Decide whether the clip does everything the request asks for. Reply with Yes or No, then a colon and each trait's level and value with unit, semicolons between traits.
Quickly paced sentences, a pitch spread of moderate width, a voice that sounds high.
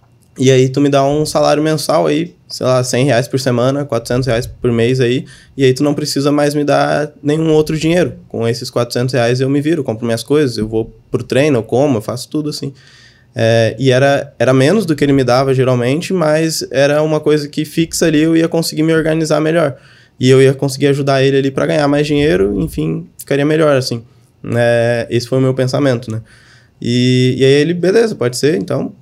No: fast, 220 wpm; average, 3.4 semitones; low, 135 Hz